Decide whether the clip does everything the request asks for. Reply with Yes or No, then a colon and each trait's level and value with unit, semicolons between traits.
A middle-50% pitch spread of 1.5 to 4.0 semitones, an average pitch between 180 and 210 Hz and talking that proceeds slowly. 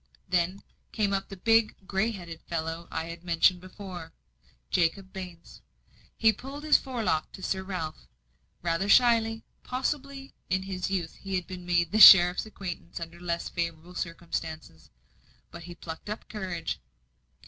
No: average, 3.4 semitones; medium, 185 Hz; average, 150 wpm